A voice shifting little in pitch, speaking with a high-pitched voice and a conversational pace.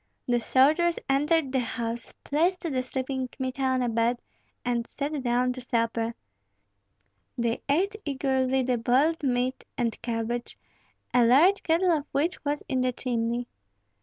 No: average, 3.1 semitones; very high, 255 Hz; average, 145 wpm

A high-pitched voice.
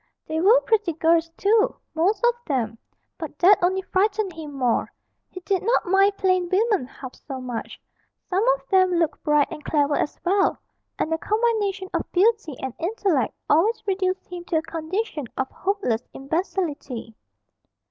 Yes: very high, 360 Hz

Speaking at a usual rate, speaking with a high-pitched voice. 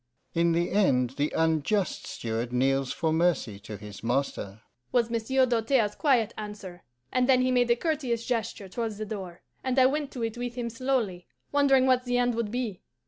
Yes: average, 190 wpm; high, 220 Hz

